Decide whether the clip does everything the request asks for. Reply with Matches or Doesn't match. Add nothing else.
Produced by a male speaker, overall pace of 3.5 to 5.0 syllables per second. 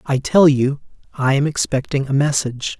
Doesn't match